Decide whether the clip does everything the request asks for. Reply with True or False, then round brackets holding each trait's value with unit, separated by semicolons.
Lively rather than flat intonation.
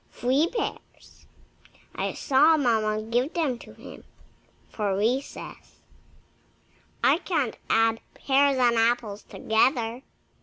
False (3.8 semitones)